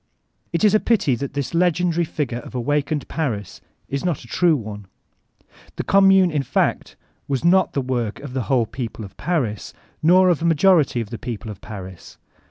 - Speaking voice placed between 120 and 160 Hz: Yes, medium, 140 Hz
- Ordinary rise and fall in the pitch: No, wide, 6.6 semitones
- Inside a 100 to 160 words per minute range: No, average, 185 wpm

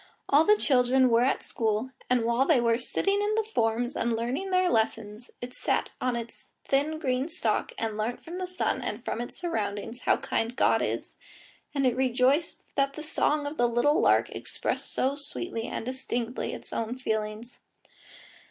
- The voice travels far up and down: No, average, 4.1 semitones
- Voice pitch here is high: Yes, very high, 250 Hz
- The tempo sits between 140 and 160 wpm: No, average, 180 wpm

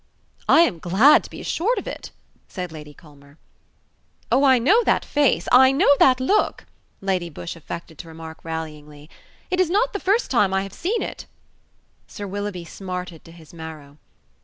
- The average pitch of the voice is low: No, medium, 185 Hz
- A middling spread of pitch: No, wide, 9.0 semitones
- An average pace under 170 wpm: No, average, 175 wpm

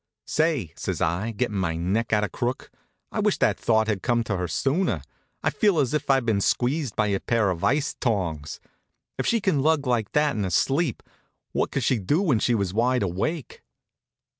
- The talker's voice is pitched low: Yes, low, 115 Hz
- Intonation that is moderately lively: No, wide, 6.2 semitones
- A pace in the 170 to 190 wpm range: No, fast, 205 wpm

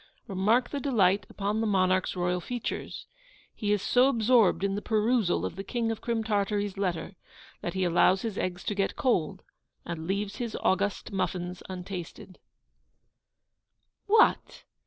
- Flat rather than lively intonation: No, average, 3.3 semitones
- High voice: Yes, high, 200 Hz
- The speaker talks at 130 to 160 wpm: Yes, average, 150 wpm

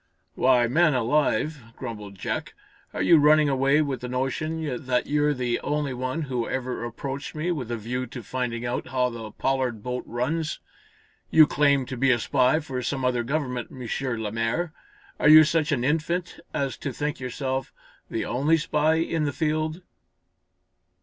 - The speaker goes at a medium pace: Yes, average, 170 wpm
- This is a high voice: No, low, 135 Hz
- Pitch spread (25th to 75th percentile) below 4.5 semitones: Yes, average, 3.5 semitones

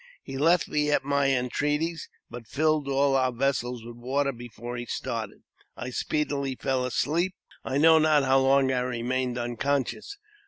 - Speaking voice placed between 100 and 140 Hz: Yes, low, 135 Hz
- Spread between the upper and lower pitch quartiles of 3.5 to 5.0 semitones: No, average, 2.9 semitones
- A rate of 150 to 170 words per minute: Yes, average, 165 wpm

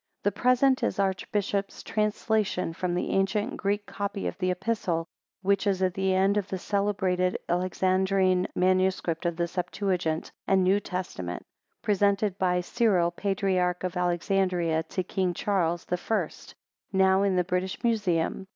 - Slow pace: No, average, 150 wpm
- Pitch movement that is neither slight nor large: No, narrow, 1.9 semitones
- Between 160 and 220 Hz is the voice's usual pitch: Yes, high, 190 Hz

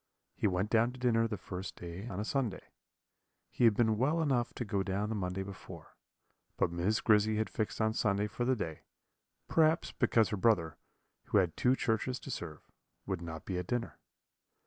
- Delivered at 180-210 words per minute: Yes, average, 190 wpm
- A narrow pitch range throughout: No, average, 4.1 semitones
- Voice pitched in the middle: No, low, 105 Hz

